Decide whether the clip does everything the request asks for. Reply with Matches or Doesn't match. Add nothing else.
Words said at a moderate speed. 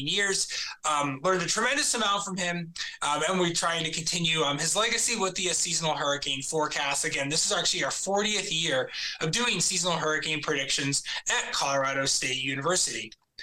Matches